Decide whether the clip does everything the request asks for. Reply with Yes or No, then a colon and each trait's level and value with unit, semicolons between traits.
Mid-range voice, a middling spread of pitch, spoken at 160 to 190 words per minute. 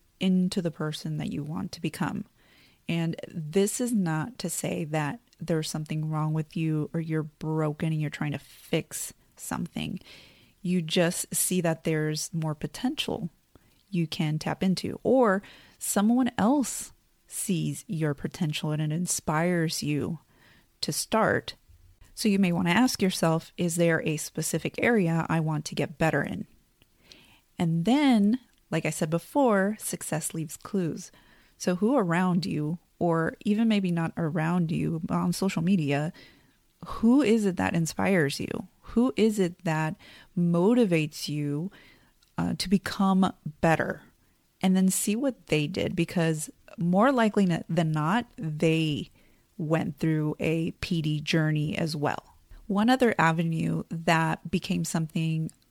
No: medium, 170 Hz; average, 3.5 semitones; average, 145 wpm